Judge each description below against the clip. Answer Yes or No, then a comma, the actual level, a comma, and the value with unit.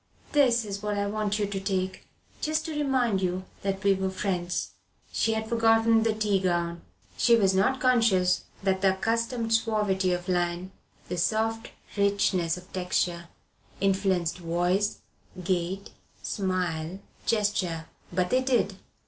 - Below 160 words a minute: Yes, average, 140 wpm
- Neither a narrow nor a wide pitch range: Yes, average, 3.5 semitones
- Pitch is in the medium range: No, high, 195 Hz